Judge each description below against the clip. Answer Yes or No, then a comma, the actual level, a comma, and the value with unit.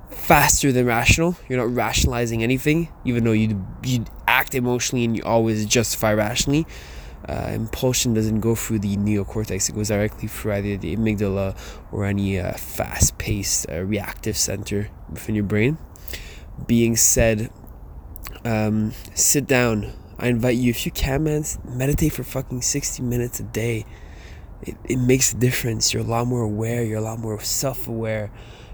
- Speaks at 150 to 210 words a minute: Yes, average, 155 wpm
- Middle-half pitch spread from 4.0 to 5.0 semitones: No, average, 3.3 semitones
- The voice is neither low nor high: No, low, 110 Hz